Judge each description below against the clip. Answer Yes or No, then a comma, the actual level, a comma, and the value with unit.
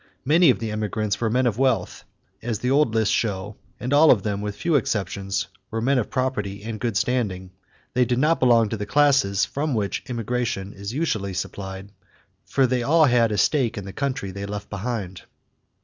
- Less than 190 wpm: No, average, 195 wpm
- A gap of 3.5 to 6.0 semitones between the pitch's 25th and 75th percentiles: Yes, average, 4.2 semitones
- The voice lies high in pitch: No, low, 115 Hz